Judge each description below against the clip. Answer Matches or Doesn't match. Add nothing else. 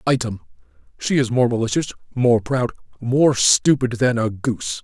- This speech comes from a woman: Doesn't match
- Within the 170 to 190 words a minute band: Doesn't match